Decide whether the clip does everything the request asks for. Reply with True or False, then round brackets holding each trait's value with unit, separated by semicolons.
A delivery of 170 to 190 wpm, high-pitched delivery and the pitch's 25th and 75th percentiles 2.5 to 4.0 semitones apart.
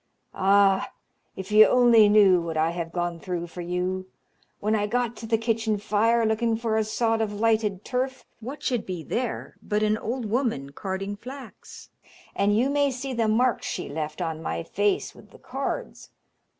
True (180 wpm; 215 Hz; 3.7 semitones)